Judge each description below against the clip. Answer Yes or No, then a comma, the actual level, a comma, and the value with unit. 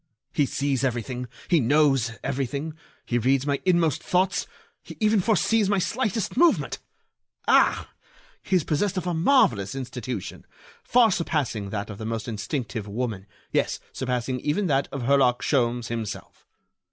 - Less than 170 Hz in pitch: Yes, low, 135 Hz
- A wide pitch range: Yes, wide, 6.7 semitones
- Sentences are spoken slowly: No, average, 145 wpm